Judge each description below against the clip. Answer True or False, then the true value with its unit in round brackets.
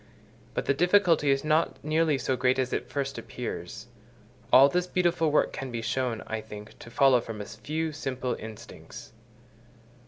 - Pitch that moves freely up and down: False (4.9 semitones)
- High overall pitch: False (135 Hz)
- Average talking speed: True (165 wpm)